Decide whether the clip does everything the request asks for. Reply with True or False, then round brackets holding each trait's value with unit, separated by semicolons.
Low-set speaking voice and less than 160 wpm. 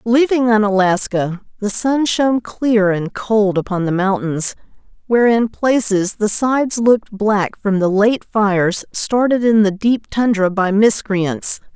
False (210 Hz; 150 wpm)